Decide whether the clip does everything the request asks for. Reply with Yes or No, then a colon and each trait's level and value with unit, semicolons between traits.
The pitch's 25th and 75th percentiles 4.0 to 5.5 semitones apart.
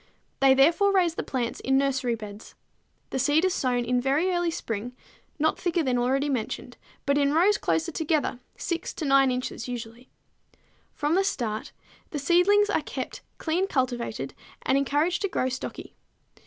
Yes: average, 5.2 semitones